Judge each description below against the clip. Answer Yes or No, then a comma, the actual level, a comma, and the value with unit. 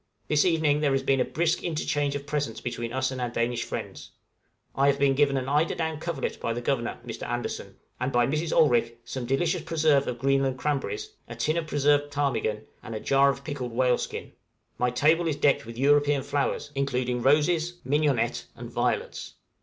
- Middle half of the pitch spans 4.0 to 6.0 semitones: No, average, 3.1 semitones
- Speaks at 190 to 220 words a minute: Yes, average, 195 wpm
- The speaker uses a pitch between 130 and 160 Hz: Yes, medium, 140 Hz